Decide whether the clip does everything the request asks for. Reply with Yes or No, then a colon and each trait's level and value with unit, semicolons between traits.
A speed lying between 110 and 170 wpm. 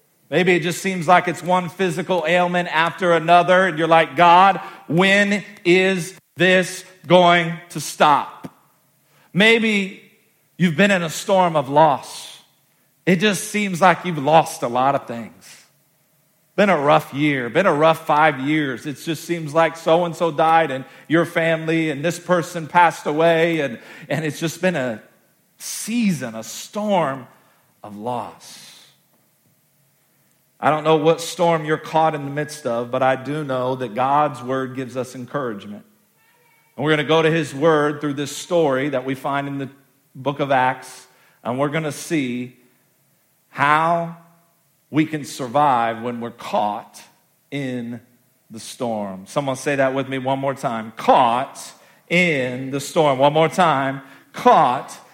Yes: average, 160 wpm